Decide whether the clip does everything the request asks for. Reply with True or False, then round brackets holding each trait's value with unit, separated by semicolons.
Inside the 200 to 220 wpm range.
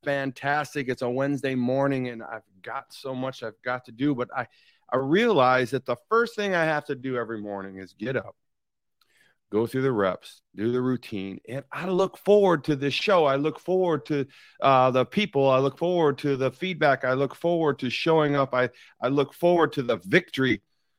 True (205 wpm)